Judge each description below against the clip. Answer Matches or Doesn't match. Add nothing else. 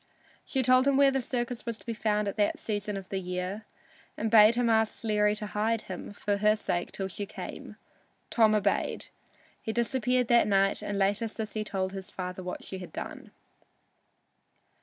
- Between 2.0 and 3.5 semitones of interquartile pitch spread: Matches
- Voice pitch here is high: Matches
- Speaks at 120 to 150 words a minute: Doesn't match